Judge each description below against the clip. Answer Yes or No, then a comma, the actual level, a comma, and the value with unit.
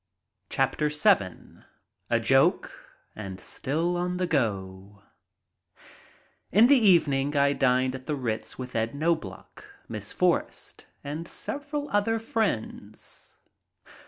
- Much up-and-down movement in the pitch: Yes, wide, 7.8 semitones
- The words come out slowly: Yes, slow, 120 wpm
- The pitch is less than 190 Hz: Yes, medium, 140 Hz